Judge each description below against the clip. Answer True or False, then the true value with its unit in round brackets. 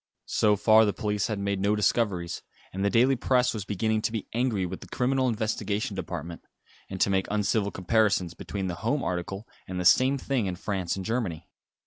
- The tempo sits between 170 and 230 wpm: True (195 wpm)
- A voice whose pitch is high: False (105 Hz)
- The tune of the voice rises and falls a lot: False (3.1 semitones)